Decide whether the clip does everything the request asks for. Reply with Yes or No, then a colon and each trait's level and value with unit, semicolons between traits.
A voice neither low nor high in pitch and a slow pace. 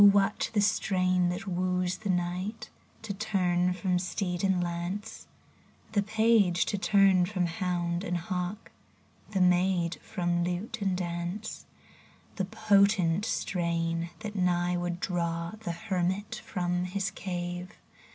Yes: medium, 180 Hz; slow, 130 wpm